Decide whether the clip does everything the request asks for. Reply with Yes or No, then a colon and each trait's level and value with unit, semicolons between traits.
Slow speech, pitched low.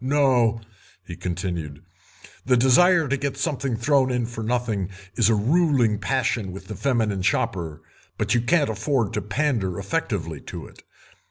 No: average, 155 wpm; low, 115 Hz